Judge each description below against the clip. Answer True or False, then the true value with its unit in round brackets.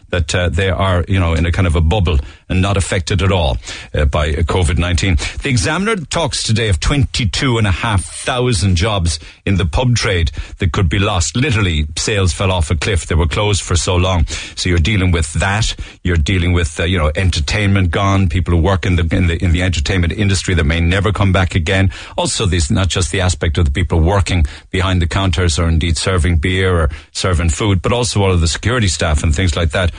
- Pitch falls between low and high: False (90 Hz)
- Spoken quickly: True (215 wpm)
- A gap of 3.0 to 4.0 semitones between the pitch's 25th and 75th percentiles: False (2.6 semitones)